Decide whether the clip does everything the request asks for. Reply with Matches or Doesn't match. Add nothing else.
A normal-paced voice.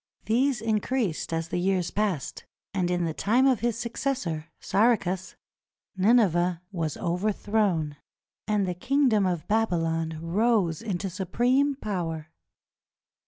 Doesn't match